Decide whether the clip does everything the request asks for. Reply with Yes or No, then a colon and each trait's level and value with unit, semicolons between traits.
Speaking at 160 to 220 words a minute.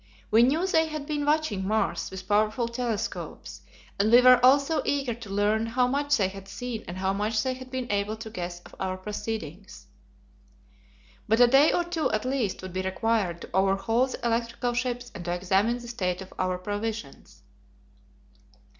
Yes: average, 180 wpm